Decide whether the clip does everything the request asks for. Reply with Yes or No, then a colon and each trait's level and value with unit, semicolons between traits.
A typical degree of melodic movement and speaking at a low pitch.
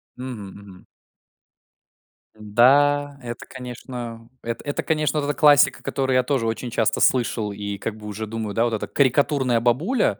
Yes: average, 4.0 semitones; low, 120 Hz